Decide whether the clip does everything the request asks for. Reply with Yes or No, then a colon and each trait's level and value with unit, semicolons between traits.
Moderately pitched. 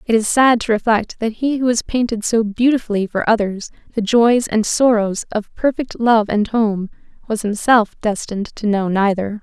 No: high, 220 Hz